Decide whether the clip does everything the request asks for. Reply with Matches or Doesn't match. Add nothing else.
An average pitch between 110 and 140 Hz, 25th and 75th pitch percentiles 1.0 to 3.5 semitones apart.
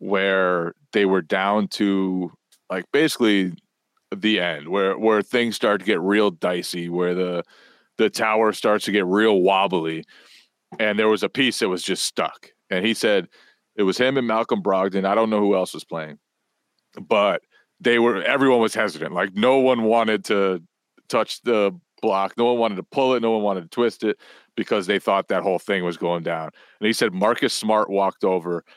Doesn't match